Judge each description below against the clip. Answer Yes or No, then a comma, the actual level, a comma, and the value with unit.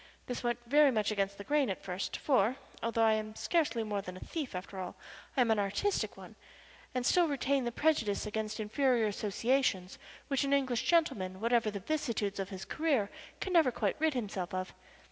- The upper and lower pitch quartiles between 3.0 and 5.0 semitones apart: No, wide, 5.5 semitones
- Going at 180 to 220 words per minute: Yes, average, 195 wpm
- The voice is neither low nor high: No, high, 230 Hz